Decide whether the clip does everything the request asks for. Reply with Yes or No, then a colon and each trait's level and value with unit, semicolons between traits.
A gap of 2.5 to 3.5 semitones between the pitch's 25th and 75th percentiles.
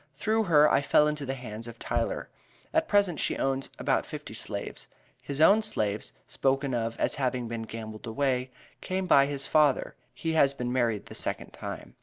No: average, 4.3 semitones